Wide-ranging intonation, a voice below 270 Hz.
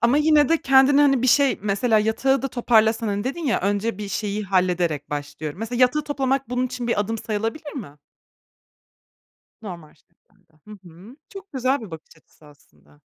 Yes: wide, 6.0 semitones; high, 225 Hz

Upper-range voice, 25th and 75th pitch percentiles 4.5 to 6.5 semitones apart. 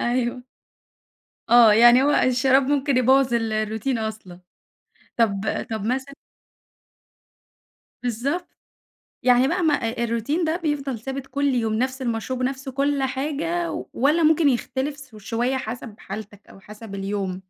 No: very high, 255 Hz; average, 3.6 semitones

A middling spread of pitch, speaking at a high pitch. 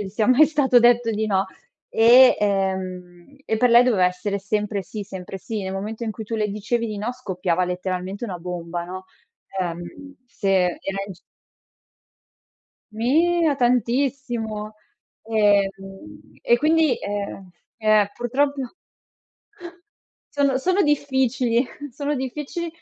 Yes: average, 4.9 semitones; high, 220 Hz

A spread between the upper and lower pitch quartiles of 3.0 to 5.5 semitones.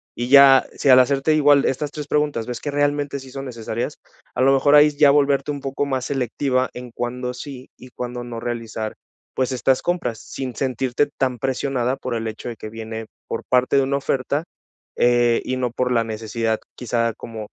No: narrow, 2.6 semitones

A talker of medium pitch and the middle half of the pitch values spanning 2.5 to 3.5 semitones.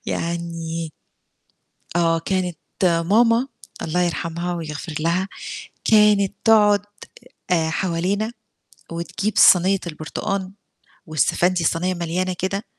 Yes: medium, 175 Hz; average, 2.8 semitones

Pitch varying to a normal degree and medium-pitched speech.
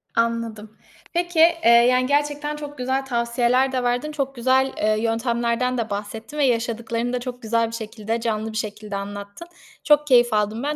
No: average, 3.1 semitones; high, 240 Hz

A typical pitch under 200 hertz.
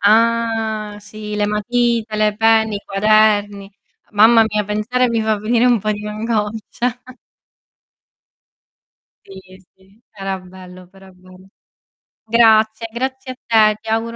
No: high, 215 Hz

